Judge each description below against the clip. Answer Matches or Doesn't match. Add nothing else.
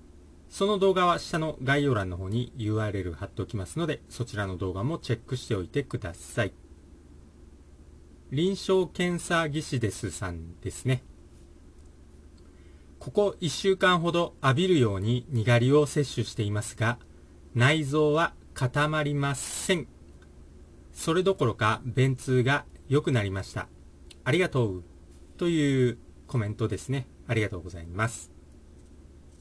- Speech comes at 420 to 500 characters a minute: Doesn't match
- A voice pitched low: Matches